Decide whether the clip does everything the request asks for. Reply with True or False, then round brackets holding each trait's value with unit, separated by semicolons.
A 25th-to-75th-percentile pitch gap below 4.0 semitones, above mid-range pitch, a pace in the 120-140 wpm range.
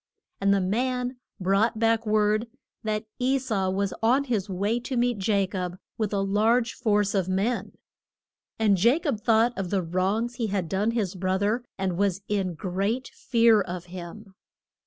False (3.3 semitones; 210 Hz; 175 wpm)